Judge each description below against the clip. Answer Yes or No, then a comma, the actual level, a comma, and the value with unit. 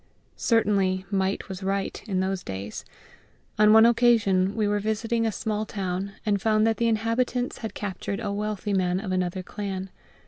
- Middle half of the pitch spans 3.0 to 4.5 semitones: No, narrow, 2.6 semitones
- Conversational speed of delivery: Yes, average, 170 wpm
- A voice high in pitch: Yes, high, 205 Hz